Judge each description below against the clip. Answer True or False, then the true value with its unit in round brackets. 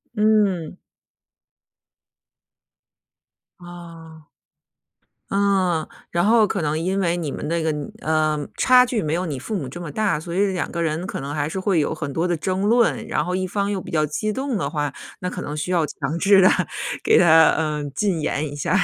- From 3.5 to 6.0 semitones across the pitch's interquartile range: True (4.0 semitones)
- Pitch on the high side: False (170 Hz)